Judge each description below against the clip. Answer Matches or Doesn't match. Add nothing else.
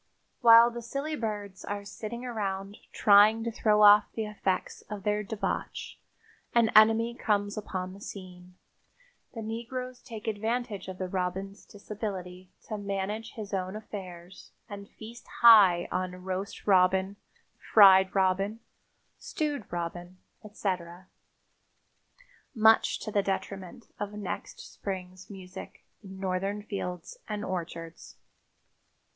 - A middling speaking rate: Doesn't match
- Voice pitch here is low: Doesn't match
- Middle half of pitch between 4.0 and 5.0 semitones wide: Doesn't match